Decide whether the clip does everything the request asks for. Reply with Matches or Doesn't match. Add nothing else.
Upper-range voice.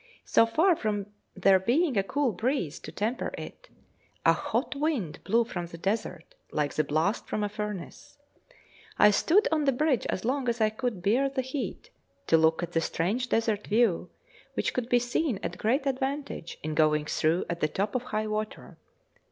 Matches